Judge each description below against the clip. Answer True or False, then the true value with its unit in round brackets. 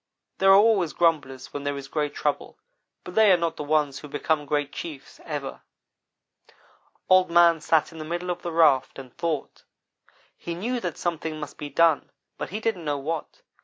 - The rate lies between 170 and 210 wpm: True (190 wpm)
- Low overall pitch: False (160 Hz)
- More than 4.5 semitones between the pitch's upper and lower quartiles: False (3.0 semitones)